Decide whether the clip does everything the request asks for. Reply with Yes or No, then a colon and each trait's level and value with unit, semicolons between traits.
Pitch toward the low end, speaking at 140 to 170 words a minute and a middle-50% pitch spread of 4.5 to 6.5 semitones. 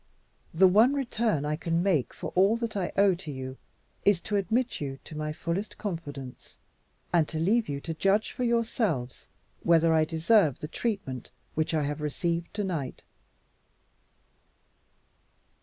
No: medium, 170 Hz; average, 155 wpm; average, 5.3 semitones